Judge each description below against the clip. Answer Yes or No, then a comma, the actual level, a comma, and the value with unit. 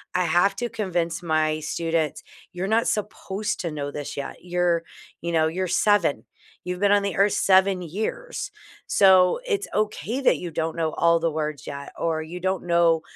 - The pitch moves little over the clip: No, average, 3.5 semitones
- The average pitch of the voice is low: No, medium, 175 Hz